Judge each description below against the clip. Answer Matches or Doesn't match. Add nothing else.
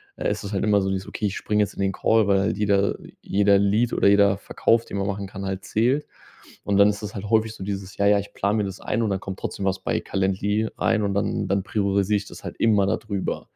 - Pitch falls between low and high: Doesn't match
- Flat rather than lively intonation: Matches